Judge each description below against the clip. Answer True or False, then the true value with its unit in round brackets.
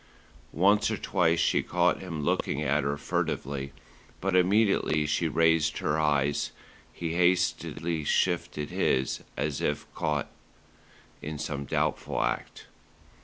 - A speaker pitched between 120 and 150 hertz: False (75 Hz)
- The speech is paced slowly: True (120 wpm)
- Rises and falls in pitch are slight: False (3.2 semitones)